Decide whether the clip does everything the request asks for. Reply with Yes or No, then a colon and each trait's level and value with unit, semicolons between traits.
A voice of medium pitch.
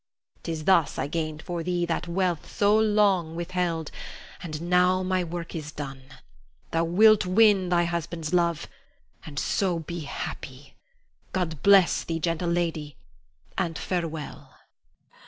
Yes: medium, 170 Hz